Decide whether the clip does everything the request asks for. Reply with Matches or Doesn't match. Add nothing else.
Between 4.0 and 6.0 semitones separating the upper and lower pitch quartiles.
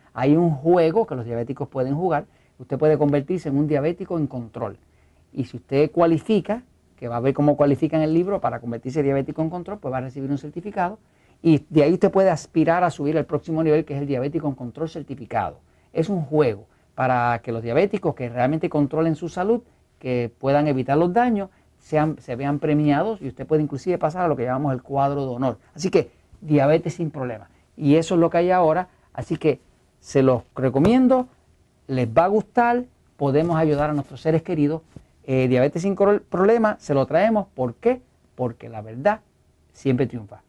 Matches